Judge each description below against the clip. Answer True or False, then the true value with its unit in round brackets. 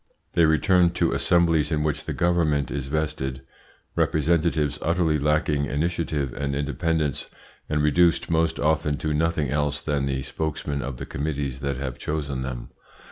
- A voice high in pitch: False (75 Hz)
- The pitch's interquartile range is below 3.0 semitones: True (2.4 semitones)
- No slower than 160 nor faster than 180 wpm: False (150 wpm)